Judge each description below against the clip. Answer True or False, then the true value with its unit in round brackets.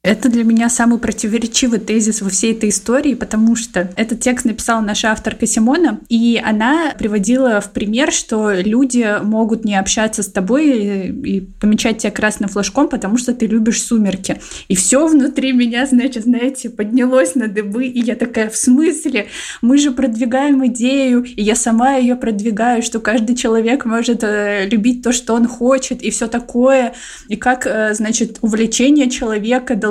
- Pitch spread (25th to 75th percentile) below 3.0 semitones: True (2.6 semitones)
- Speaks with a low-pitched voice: False (235 Hz)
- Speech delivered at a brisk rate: True (165 wpm)